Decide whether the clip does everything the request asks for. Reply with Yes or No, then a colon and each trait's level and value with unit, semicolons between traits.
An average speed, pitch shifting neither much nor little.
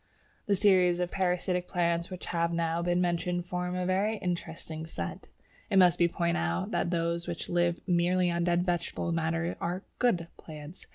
No: average, 175 wpm; narrow, 1.1 semitones